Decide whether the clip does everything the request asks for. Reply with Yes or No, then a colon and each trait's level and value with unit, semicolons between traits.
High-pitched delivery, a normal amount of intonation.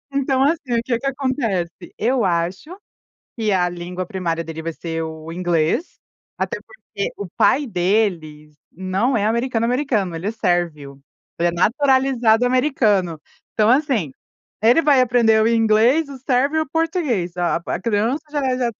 No: high, 220 Hz; wide, 6.8 semitones